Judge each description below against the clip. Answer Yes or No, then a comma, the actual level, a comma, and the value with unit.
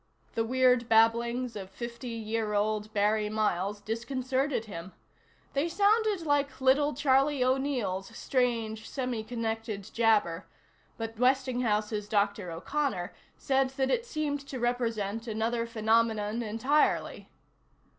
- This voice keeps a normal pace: No, slow, 115 wpm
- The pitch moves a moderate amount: Yes, average, 3.5 semitones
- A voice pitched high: Yes, high, 230 Hz